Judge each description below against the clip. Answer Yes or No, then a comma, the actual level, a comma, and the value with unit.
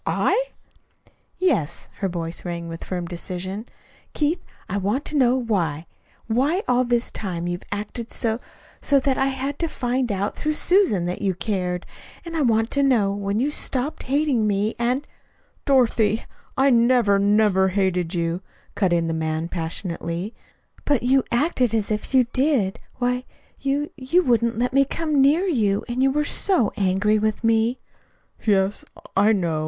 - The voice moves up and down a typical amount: No, wide, 5.8 semitones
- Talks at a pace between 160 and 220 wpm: Yes, average, 165 wpm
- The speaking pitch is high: Yes, high, 225 Hz